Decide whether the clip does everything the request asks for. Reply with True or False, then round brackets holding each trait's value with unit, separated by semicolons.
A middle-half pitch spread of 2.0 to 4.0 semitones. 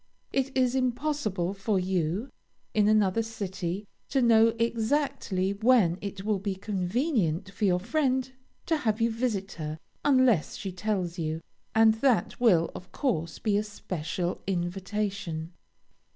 False (4.5 semitones)